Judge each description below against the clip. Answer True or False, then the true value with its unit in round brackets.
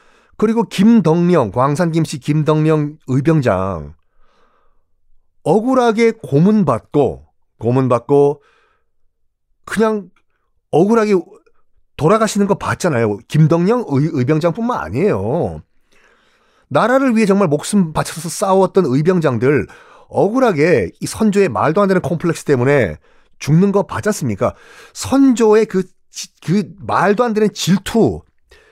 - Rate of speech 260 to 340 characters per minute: False (240 characters per minute)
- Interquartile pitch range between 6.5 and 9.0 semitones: True (6.9 semitones)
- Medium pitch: True (175 Hz)